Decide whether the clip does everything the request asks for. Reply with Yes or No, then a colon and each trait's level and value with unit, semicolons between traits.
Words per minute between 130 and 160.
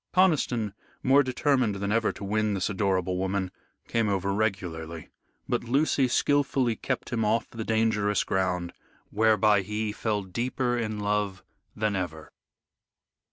Yes: slow, 135 wpm